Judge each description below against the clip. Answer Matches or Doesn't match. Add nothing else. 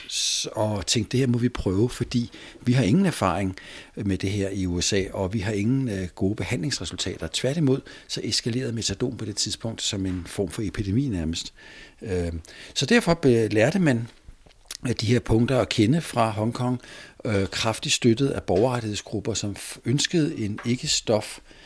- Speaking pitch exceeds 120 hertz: Doesn't match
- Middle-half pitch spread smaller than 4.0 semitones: Doesn't match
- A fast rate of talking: Doesn't match